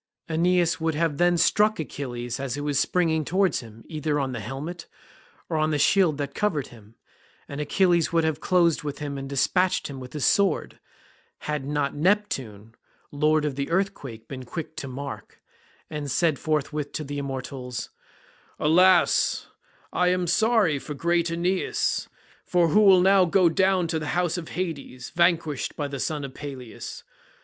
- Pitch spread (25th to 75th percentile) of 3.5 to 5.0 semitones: Yes, average, 4.0 semitones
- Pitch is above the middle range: No, medium, 155 Hz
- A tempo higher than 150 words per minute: Yes, average, 165 wpm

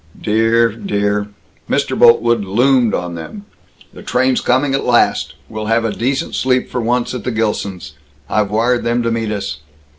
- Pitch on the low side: Yes, low, 115 Hz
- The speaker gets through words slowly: No, average, 175 wpm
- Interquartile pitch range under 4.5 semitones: Yes, average, 2.9 semitones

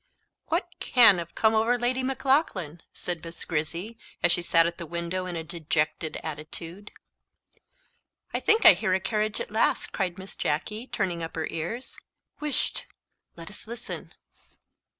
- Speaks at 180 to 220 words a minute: No, average, 155 wpm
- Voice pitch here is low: No, medium, 185 Hz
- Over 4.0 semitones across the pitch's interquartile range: Yes, average, 5.2 semitones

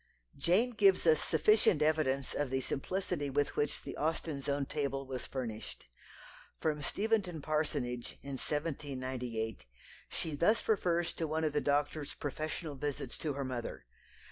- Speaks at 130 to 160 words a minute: Yes, average, 145 wpm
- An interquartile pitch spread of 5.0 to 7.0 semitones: No, average, 3.0 semitones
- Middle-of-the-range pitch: Yes, medium, 145 Hz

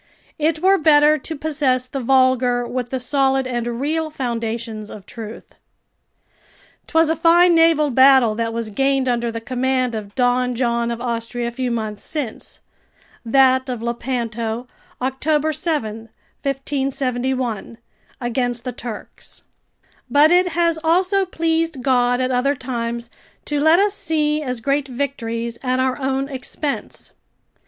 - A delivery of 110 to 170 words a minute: Yes, average, 140 wpm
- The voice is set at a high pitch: Yes, very high, 260 Hz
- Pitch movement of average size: Yes, average, 3.7 semitones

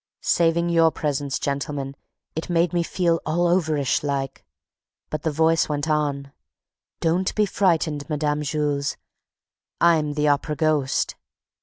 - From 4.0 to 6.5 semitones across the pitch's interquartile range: No, narrow, 2.5 semitones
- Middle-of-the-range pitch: Yes, medium, 155 Hz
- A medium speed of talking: No, slow, 130 wpm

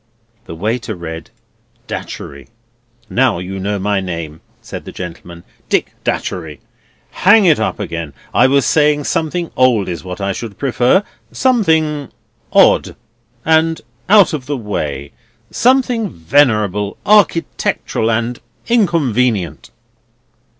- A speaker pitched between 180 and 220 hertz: No, low, 120 Hz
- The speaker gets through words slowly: Yes, slow, 115 wpm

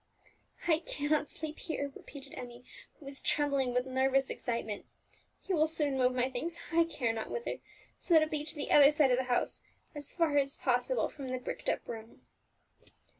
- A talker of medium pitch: No, very high, 280 Hz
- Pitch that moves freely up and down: No, average, 3.4 semitones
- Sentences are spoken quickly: No, average, 190 wpm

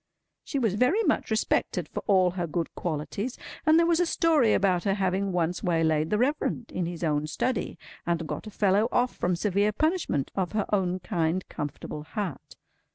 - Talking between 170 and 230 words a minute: Yes, average, 185 wpm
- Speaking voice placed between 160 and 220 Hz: Yes, high, 190 Hz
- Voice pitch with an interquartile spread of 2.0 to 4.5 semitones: No, average, 5.0 semitones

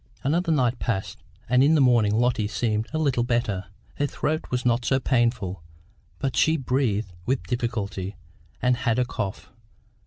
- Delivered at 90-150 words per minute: No, average, 160 wpm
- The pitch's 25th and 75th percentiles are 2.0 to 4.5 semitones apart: Yes, average, 3.6 semitones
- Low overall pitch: Yes, low, 120 Hz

